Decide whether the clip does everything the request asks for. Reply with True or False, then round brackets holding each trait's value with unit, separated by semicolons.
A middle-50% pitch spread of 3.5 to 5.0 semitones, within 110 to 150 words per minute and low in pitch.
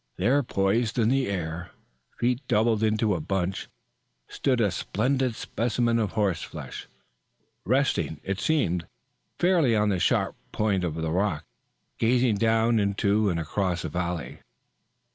True (4.5 semitones; 140 wpm; 105 Hz)